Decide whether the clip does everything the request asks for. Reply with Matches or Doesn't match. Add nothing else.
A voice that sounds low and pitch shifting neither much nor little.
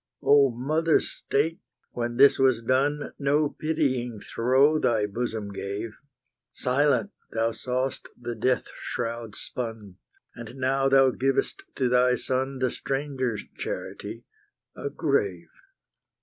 Matches